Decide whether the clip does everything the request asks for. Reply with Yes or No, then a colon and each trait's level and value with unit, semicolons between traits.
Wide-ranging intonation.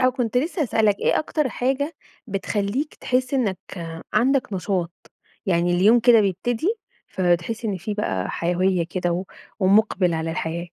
Yes: wide, 5.8 semitones